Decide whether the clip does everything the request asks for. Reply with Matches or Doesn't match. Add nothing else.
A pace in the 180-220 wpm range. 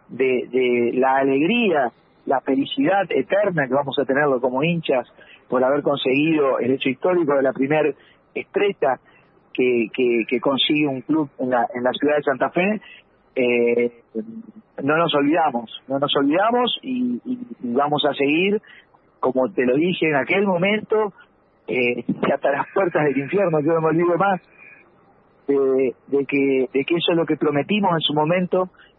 Doesn't match